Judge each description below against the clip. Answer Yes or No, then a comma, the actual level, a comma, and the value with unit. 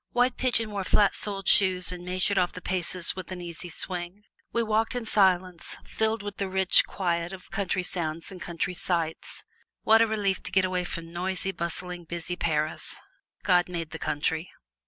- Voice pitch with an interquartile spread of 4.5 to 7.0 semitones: No, narrow, 2.4 semitones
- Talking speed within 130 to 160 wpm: No, average, 180 wpm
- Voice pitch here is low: No, medium, 185 Hz